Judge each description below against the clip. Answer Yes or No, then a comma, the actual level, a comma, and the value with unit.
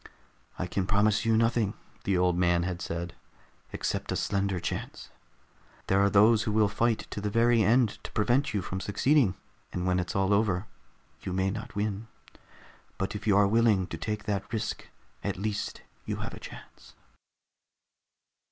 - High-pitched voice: No, low, 100 Hz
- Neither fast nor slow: Yes, average, 170 wpm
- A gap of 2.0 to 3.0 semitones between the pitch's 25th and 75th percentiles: Yes, average, 2.7 semitones